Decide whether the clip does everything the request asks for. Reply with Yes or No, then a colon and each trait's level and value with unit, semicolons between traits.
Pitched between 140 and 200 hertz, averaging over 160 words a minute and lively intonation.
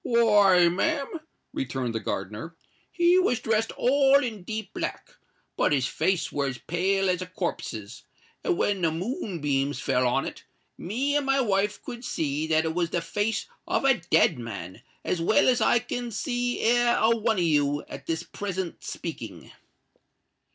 Yes: high, 190 Hz; average, 170 wpm; wide, 7.2 semitones